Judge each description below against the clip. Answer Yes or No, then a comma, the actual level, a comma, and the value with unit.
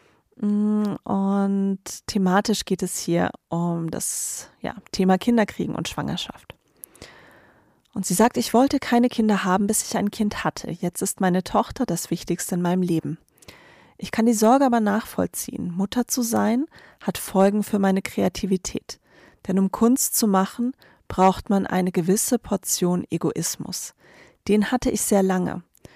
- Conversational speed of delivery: Yes, average, 150 wpm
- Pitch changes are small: No, average, 3.3 semitones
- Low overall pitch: No, high, 195 Hz